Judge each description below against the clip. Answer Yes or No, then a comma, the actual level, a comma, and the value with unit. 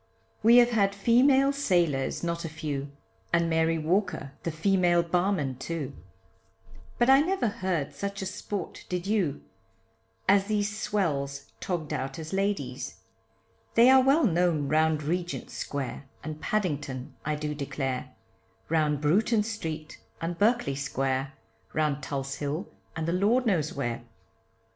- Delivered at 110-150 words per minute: Yes, average, 140 wpm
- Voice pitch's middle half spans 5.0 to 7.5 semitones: Yes, wide, 5.5 semitones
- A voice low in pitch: No, medium, 170 Hz